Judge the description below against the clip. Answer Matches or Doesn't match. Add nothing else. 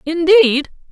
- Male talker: Doesn't match